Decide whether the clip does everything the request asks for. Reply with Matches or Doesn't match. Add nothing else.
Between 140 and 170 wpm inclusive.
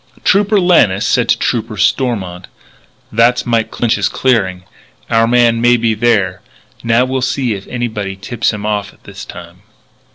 Matches